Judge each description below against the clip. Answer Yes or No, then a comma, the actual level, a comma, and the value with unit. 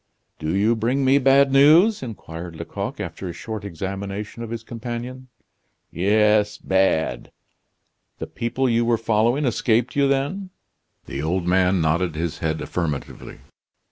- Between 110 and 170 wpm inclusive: Yes, average, 140 wpm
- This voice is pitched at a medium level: No, low, 110 Hz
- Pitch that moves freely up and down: Yes, wide, 6.0 semitones